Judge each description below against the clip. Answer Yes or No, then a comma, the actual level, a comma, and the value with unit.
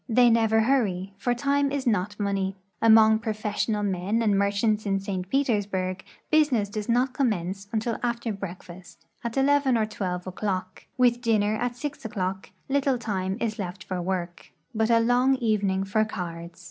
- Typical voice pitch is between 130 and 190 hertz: No, high, 215 Hz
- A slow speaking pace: No, average, 165 wpm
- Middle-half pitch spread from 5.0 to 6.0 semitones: No, average, 3.8 semitones